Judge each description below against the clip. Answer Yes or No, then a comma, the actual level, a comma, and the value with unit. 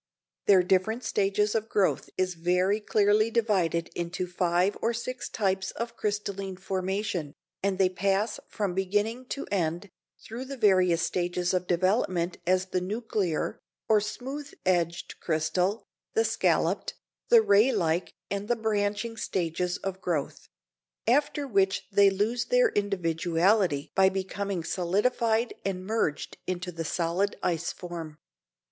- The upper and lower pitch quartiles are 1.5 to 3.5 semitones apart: Yes, average, 3.2 semitones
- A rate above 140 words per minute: No, slow, 135 wpm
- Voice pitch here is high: Yes, high, 195 Hz